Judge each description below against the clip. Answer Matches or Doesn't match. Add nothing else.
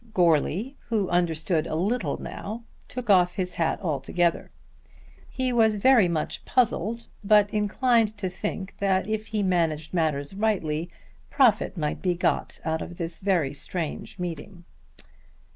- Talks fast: Doesn't match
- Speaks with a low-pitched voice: Doesn't match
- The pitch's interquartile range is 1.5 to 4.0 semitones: Doesn't match